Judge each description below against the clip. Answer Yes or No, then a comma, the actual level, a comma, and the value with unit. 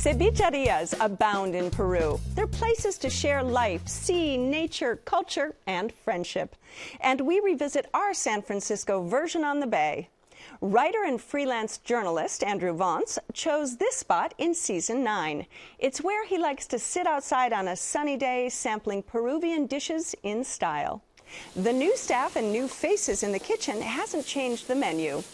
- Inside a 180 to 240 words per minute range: No, average, 155 wpm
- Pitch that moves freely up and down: Yes, wide, 6.9 semitones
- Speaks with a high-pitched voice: Yes, very high, 270 Hz